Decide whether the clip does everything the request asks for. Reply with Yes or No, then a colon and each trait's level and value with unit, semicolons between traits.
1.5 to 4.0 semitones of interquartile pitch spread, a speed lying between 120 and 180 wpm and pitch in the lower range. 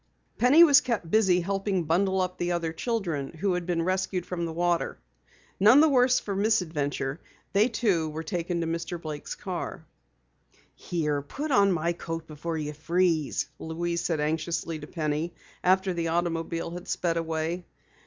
No: average, 2.8 semitones; average, 165 wpm; medium, 170 Hz